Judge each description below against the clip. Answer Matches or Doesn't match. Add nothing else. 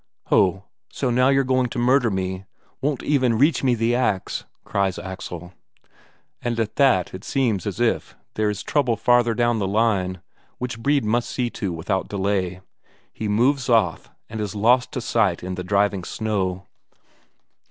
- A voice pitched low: Matches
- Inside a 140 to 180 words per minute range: Matches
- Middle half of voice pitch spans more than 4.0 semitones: Matches